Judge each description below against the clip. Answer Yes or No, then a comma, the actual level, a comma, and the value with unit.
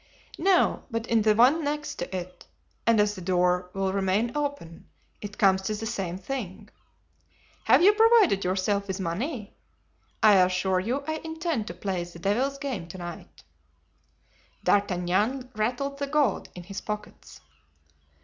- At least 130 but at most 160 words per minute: Yes, average, 150 wpm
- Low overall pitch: No, high, 210 Hz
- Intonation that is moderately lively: No, wide, 6.6 semitones